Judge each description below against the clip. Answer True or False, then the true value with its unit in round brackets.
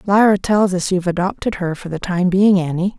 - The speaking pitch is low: False (185 Hz)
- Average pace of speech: False (220 wpm)